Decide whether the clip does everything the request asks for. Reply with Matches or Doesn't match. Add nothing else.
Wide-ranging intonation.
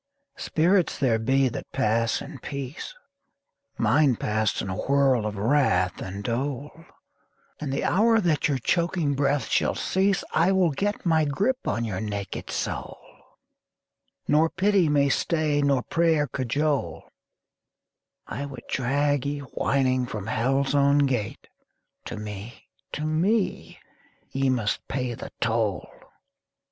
Doesn't match